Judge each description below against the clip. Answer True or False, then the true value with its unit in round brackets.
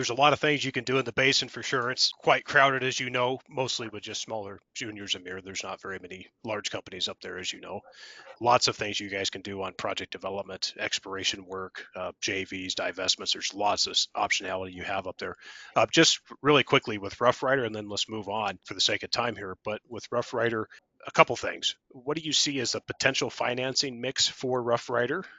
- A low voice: True (115 Hz)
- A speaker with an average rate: False (225 wpm)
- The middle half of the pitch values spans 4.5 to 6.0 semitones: True (5.1 semitones)